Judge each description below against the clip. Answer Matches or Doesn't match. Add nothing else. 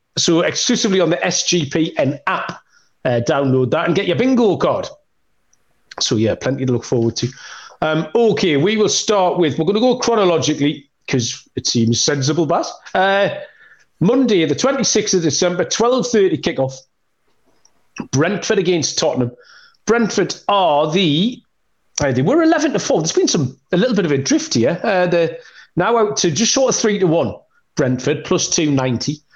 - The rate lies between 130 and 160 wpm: Doesn't match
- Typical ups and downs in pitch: Doesn't match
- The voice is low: Doesn't match